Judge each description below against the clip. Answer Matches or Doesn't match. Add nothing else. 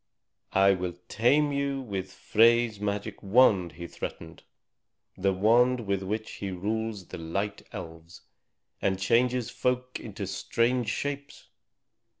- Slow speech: Matches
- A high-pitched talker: Doesn't match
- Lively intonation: Doesn't match